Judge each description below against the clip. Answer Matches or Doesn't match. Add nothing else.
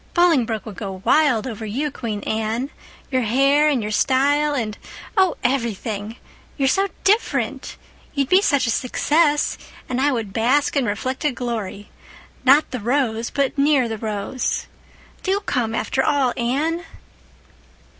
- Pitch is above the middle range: Matches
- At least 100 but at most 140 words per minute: Matches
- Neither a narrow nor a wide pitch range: Matches